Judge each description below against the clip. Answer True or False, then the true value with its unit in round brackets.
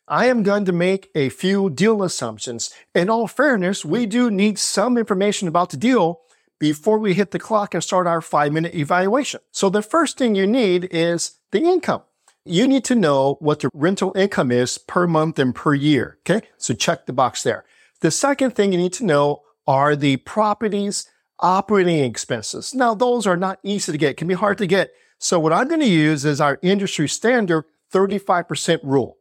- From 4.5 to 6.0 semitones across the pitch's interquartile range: True (5.2 semitones)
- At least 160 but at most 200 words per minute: True (195 wpm)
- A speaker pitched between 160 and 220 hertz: True (185 Hz)